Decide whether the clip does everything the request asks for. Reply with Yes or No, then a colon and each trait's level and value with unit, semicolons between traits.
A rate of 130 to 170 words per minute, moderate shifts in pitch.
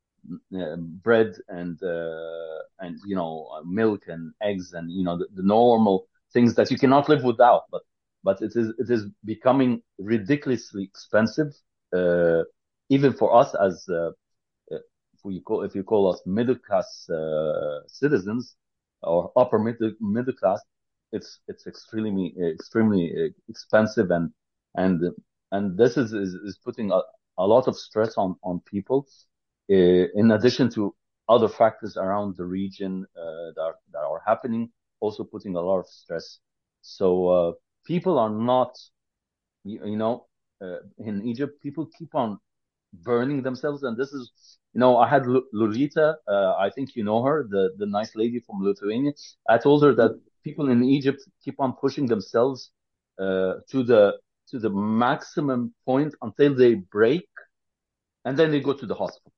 No: average, 160 wpm; wide, 5.9 semitones